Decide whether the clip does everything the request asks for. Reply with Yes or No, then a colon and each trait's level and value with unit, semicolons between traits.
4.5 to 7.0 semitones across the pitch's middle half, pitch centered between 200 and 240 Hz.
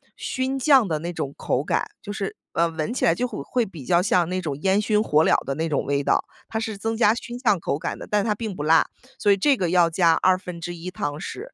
No: average, 5.2 semitones; medium, 185 Hz